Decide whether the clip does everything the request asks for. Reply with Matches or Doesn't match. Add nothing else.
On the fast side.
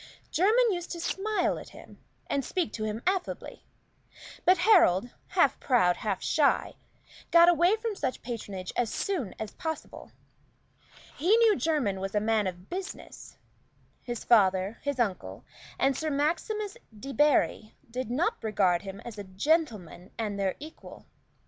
Doesn't match